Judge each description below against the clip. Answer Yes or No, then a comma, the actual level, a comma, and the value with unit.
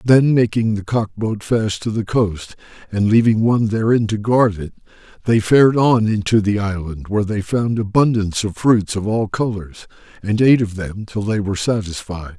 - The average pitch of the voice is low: Yes, low, 105 Hz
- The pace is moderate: Yes, average, 190 wpm